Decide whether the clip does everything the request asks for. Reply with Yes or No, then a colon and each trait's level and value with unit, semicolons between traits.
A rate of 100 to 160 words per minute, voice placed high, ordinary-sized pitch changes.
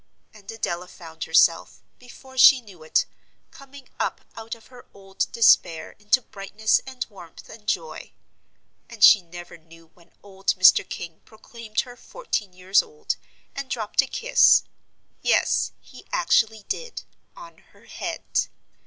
No: average, 145 wpm; high, 215 Hz; wide, 5.7 semitones